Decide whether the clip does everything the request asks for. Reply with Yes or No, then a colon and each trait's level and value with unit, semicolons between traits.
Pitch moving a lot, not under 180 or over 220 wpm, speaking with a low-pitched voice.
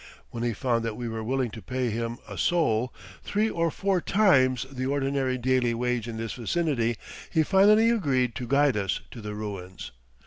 No: average, 3.8 semitones; average, 185 wpm; low, 125 Hz